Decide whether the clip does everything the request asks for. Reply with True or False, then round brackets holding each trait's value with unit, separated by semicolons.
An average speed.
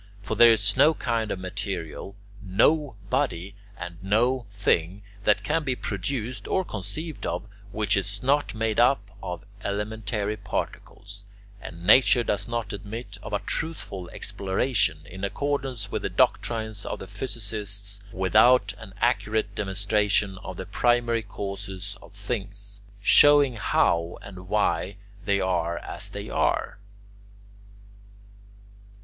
False (130 wpm)